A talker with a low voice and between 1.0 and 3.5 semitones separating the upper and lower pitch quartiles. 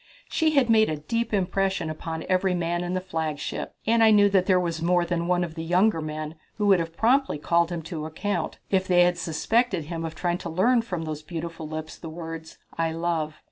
No: medium, 175 Hz; average, 3.0 semitones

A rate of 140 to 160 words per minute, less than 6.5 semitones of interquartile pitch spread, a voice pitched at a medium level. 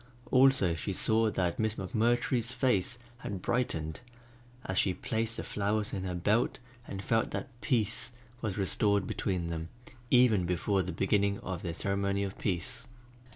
No: average, 155 wpm; average, 3.6 semitones; low, 100 Hz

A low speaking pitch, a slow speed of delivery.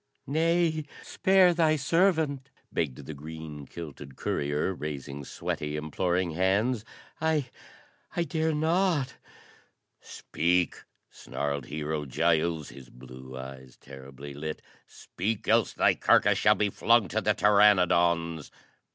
Yes: very low, 85 Hz; slow, 115 wpm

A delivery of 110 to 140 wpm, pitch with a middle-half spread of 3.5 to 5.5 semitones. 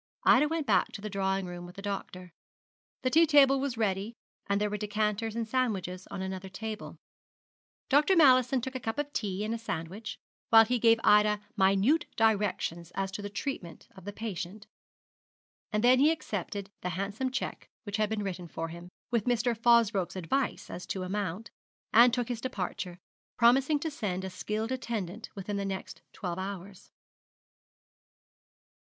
No: average, 170 wpm; average, 4.0 semitones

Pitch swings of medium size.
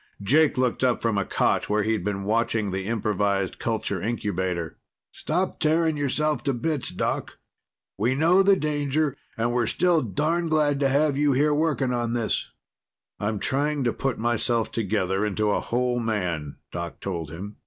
No: wide, 6.1 semitones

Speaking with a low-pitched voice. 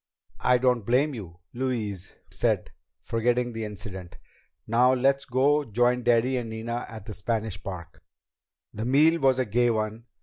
Yes: low, 120 Hz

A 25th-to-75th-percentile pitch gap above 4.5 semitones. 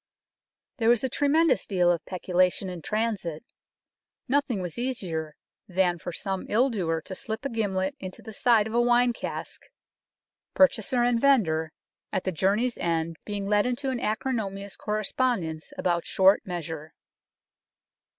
Yes: average, 5.2 semitones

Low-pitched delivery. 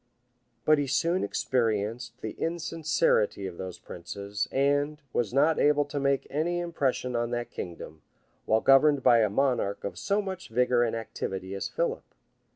Yes: low, 125 Hz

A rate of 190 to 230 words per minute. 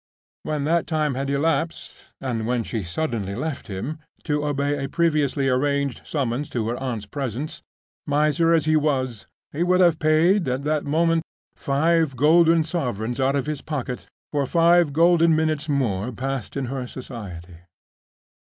No: average, 150 wpm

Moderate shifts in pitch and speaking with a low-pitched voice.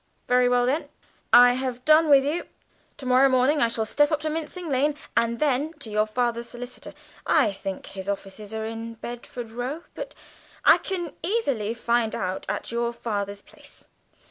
No: average, 4.4 semitones; high, 245 Hz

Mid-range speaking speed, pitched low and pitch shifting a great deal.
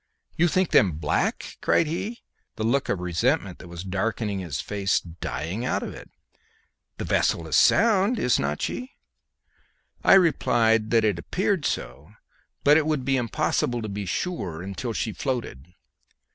Yes: average, 160 wpm; low, 115 Hz; wide, 8.7 semitones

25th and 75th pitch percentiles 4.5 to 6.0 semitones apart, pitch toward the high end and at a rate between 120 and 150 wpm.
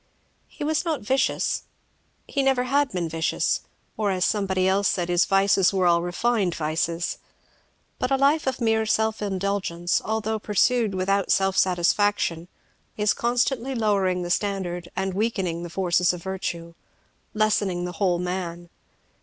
No: average, 3.8 semitones; high, 195 Hz; average, 145 wpm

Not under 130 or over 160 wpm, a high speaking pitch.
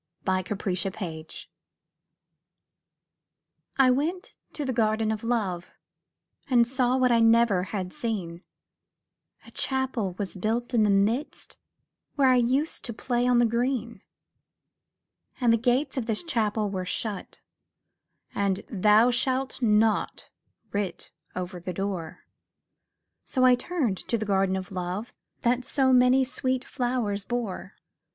Yes: slow, 135 wpm; high, 230 Hz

